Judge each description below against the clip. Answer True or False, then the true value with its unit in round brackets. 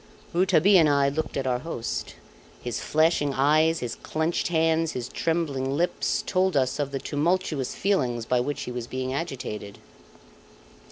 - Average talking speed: True (155 wpm)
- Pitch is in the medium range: True (145 Hz)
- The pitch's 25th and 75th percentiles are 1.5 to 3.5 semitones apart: False (4.1 semitones)